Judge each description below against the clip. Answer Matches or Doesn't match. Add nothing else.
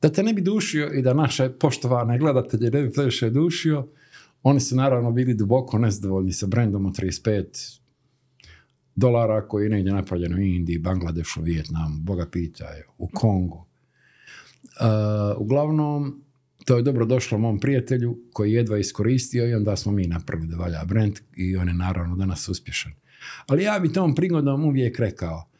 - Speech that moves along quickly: Matches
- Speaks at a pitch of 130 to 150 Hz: Doesn't match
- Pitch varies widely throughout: Matches